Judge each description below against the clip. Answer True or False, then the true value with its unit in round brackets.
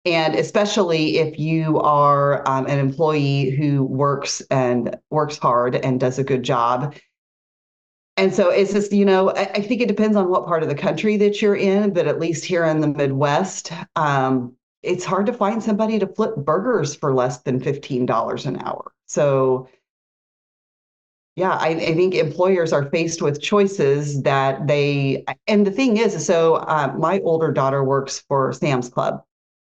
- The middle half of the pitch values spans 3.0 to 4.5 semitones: False (5.6 semitones)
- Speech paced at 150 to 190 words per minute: True (170 wpm)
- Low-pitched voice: False (155 Hz)